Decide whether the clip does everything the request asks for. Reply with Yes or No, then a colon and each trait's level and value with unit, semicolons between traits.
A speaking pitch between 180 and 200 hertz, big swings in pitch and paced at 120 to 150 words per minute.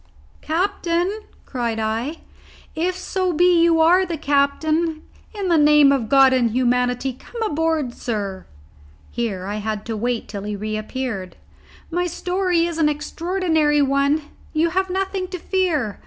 No: very high, 300 Hz; wide, 6.3 semitones; average, 145 wpm